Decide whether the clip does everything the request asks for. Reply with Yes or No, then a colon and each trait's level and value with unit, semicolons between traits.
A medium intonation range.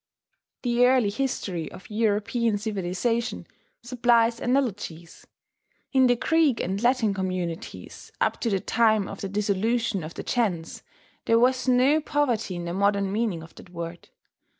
Yes: average, 4.3 semitones